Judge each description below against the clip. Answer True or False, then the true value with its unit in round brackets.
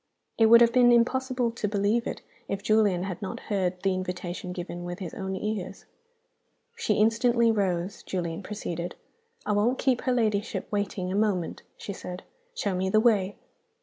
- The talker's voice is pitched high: True (205 Hz)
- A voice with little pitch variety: False (3.7 semitones)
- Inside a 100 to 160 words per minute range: False (170 wpm)